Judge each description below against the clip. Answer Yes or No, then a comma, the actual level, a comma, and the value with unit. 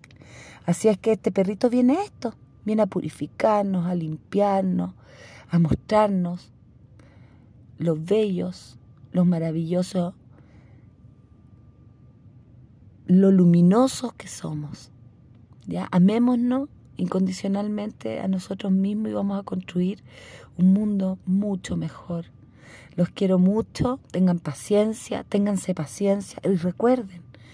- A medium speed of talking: No, slow, 100 wpm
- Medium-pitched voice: Yes, medium, 180 Hz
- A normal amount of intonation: No, wide, 8.2 semitones